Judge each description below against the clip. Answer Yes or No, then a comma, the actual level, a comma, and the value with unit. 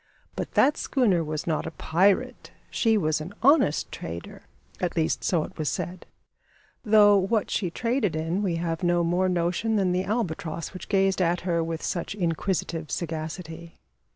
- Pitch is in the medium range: Yes, medium, 175 Hz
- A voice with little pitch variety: No, average, 3.4 semitones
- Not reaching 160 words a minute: No, average, 165 wpm